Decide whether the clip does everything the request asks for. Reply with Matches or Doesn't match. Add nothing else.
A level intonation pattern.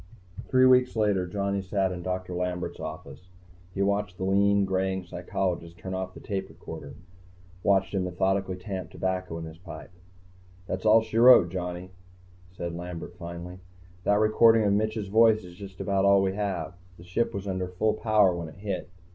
Matches